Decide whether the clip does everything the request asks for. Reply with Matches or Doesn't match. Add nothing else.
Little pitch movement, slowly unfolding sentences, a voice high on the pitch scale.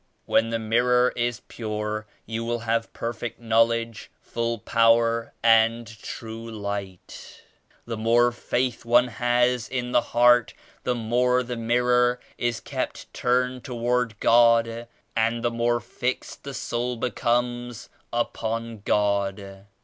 Doesn't match